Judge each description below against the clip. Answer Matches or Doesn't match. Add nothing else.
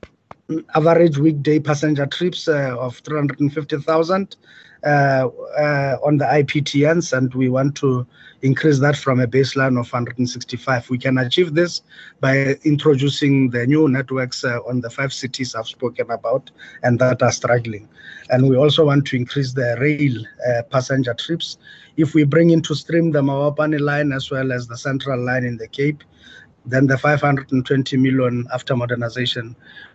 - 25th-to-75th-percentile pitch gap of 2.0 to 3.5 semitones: Matches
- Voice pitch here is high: Doesn't match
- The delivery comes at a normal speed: Matches